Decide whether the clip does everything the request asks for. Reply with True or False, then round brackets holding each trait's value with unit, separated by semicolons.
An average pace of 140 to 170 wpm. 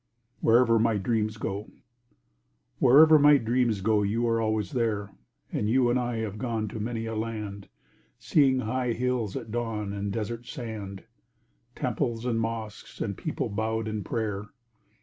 True (150 wpm)